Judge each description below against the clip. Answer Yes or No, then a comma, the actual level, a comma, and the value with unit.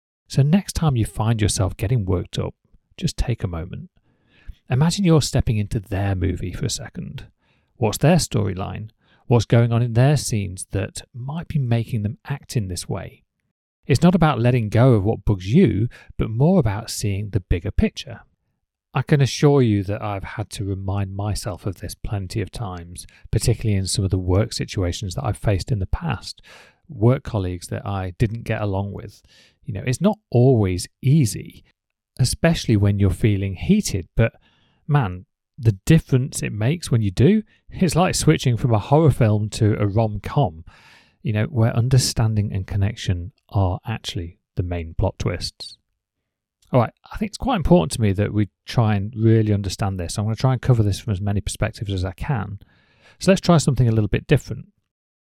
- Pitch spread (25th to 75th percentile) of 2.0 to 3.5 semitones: No, average, 4.7 semitones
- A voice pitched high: No, low, 110 Hz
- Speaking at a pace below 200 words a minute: Yes, average, 185 wpm